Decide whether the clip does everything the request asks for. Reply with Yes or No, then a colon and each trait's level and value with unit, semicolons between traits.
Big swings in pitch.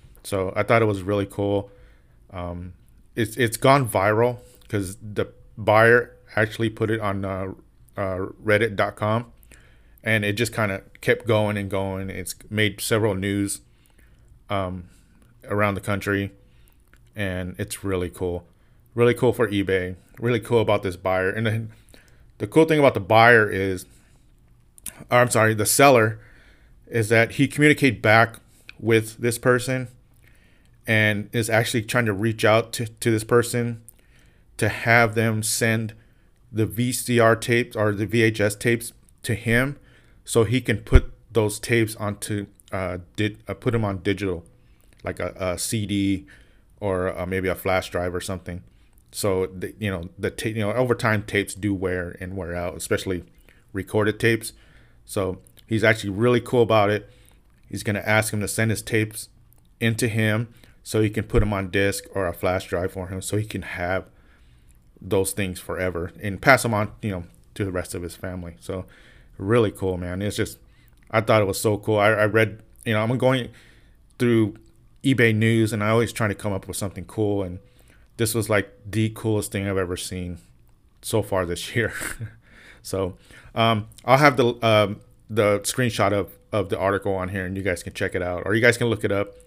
No: average, 3.1 semitones